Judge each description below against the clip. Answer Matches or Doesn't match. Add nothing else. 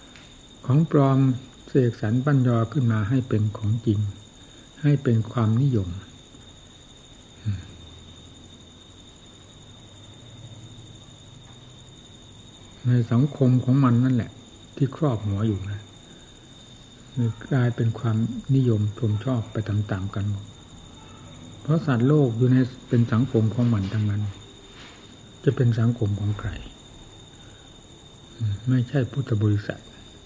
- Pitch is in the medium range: Doesn't match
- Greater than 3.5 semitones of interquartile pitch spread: Doesn't match